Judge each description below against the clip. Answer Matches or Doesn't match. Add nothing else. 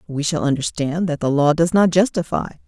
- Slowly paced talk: Doesn't match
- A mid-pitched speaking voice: Matches